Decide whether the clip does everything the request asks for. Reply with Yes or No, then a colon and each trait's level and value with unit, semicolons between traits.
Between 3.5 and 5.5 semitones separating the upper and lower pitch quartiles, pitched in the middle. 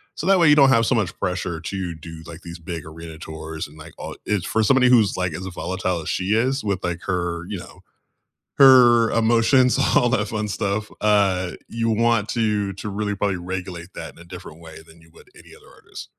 No: average, 4.9 semitones; very low, 95 Hz